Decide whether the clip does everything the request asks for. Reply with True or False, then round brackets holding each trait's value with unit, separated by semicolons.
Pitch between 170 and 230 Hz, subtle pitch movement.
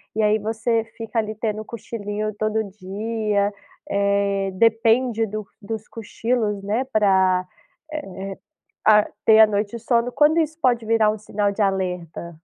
True (215 Hz; 2.0 semitones)